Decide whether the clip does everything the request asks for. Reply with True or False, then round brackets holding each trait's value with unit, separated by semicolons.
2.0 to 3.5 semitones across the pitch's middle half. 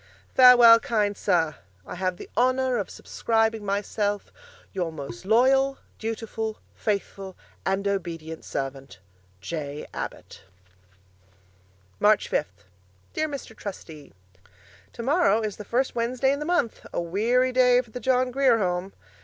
False (5.3 semitones)